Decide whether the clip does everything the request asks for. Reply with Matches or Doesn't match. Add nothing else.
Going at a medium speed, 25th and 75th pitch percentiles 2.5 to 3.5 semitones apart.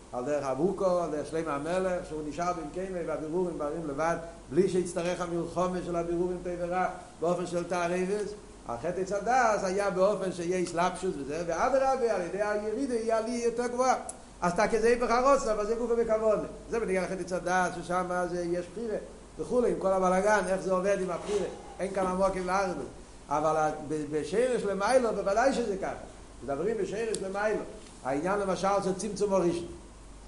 Doesn't match